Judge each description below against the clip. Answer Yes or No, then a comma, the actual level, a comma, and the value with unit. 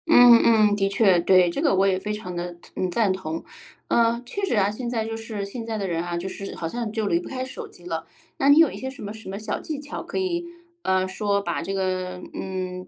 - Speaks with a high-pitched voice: Yes, high, 205 Hz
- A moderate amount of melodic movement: Yes, average, 4.2 semitones